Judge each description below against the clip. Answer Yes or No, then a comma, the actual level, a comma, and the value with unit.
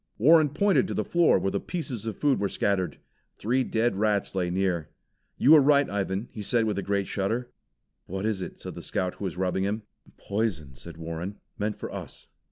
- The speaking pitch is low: Yes, low, 100 Hz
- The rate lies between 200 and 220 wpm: Yes, fast, 205 wpm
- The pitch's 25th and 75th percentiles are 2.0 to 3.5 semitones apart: No, average, 4.3 semitones